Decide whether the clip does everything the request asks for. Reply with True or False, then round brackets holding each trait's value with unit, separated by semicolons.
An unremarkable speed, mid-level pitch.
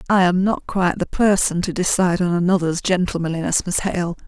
True (180 wpm; 180 Hz)